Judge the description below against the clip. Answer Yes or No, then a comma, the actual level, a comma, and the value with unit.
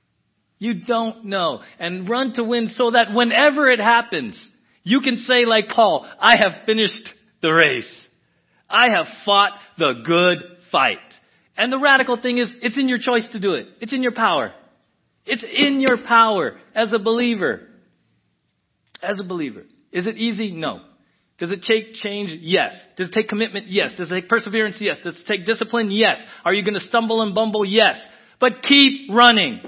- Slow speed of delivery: No, average, 180 wpm